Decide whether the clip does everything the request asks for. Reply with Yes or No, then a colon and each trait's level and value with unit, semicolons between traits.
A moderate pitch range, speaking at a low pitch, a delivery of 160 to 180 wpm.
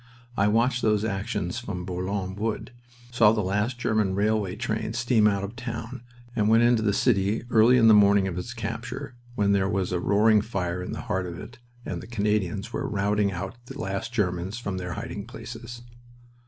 No: average, 3.0 semitones; low, 105 Hz; average, 195 wpm